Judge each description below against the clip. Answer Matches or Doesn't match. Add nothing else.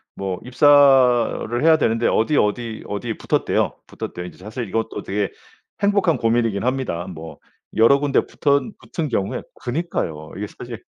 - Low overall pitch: Matches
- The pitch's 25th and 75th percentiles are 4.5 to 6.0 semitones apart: Matches